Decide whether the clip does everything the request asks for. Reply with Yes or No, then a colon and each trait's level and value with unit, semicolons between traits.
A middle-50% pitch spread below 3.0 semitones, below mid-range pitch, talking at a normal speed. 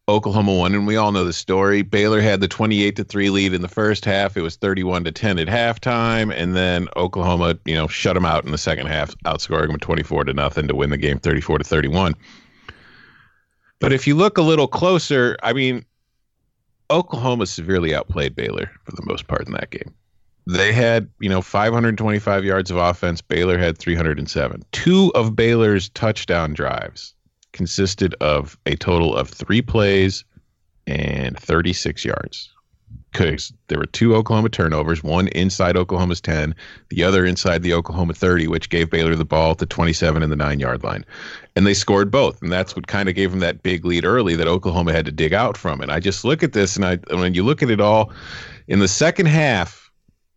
No: average, 4.2 semitones; very low, 95 Hz; average, 195 wpm